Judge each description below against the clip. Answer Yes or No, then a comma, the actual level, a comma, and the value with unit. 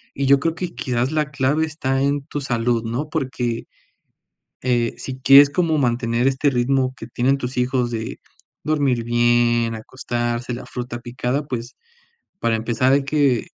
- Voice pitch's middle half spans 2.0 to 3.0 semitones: Yes, average, 2.7 semitones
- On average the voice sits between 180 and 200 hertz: No, low, 130 Hz